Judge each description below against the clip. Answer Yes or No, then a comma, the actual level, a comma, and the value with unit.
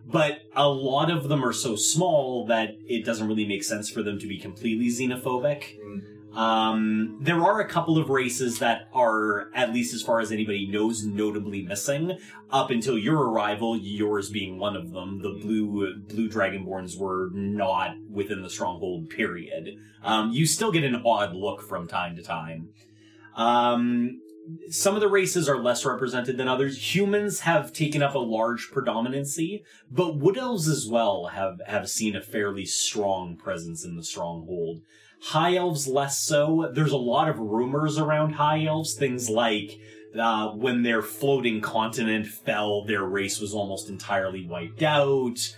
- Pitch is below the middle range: Yes, low, 115 Hz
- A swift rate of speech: No, average, 165 wpm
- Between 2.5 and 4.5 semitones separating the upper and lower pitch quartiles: No, average, 5.2 semitones